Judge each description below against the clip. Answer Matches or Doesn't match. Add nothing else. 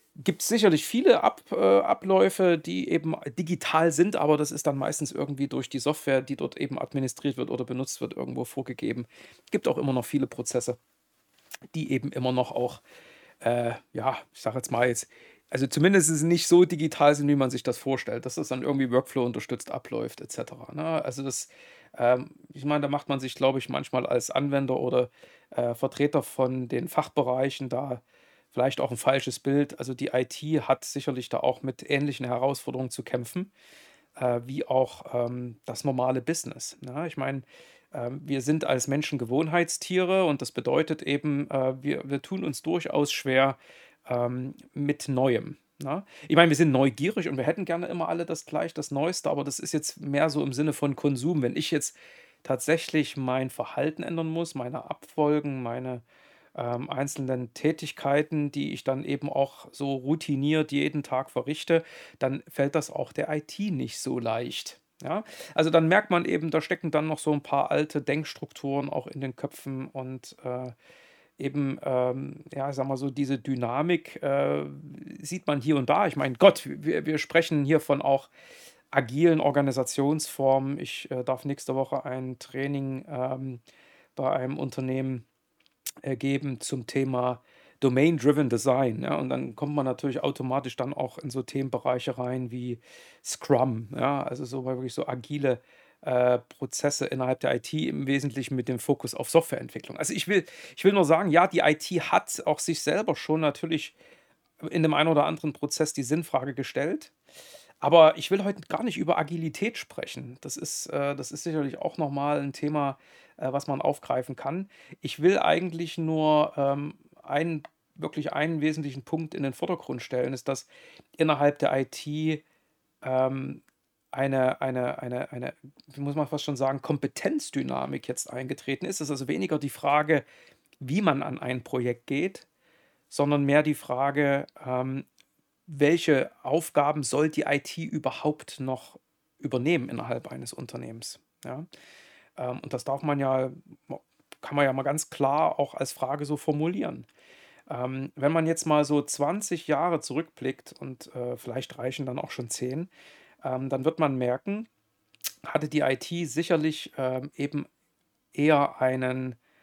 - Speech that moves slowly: Doesn't match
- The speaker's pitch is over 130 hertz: Matches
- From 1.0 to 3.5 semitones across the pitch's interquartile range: Matches